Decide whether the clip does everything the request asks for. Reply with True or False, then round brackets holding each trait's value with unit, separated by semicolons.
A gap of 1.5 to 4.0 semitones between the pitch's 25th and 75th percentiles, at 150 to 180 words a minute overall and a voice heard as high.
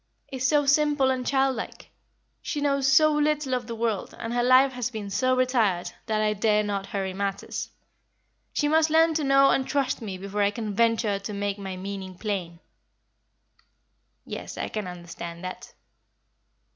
False (5.3 semitones; 170 wpm; 230 Hz)